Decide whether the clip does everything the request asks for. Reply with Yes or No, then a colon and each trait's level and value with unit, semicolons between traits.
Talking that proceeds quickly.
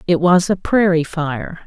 No: average, 180 wpm